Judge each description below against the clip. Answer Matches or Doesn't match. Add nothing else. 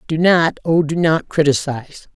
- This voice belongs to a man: Doesn't match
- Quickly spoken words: Doesn't match